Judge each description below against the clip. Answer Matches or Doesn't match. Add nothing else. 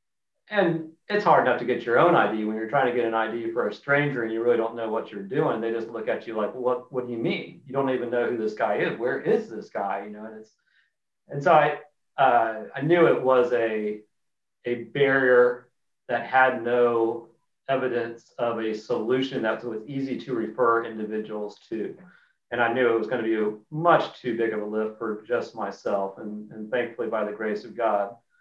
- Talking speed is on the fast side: Matches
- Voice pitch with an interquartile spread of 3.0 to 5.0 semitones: Matches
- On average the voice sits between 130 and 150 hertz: Doesn't match